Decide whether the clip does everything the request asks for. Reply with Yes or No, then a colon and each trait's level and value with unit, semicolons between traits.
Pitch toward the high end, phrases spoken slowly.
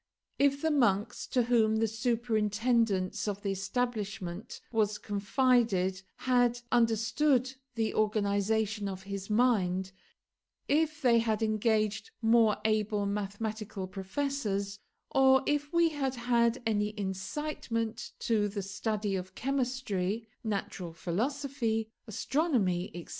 Yes: high, 220 Hz; slow, 110 wpm